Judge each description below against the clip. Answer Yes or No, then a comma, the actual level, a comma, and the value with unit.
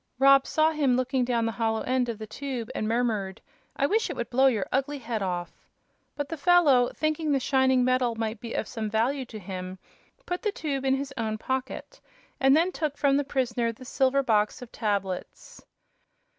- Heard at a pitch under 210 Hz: No, very high, 255 Hz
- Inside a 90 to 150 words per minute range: No, average, 200 wpm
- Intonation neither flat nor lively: Yes, average, 3.7 semitones